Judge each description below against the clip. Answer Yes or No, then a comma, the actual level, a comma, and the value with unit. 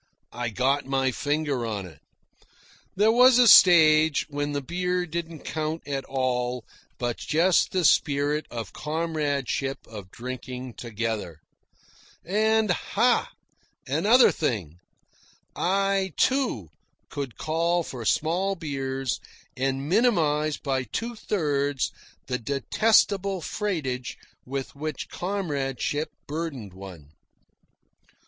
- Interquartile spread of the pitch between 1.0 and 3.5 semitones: No, wide, 5.6 semitones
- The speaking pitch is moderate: Yes, medium, 145 Hz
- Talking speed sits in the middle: No, slow, 105 wpm